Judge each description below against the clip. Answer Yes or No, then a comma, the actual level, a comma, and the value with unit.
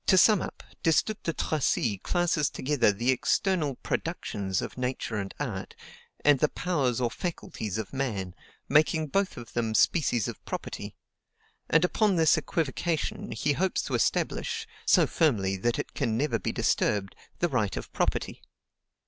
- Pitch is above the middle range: No, low, 135 Hz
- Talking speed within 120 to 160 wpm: Yes, average, 155 wpm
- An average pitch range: No, wide, 6.8 semitones